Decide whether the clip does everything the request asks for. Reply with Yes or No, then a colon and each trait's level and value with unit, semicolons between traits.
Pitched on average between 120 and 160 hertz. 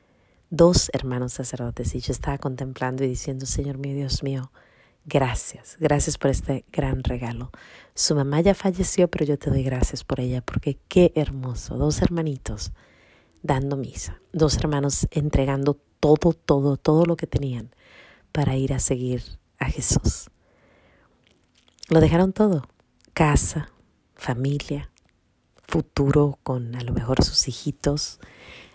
Yes: low, 135 Hz